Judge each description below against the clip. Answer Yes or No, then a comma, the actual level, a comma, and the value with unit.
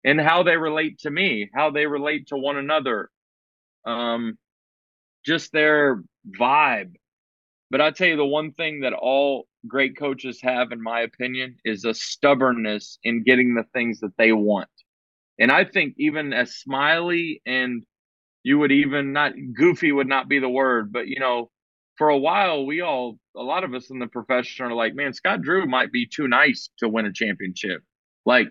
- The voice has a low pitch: Yes, low, 130 Hz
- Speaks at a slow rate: No, average, 185 wpm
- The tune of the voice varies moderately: Yes, average, 4.1 semitones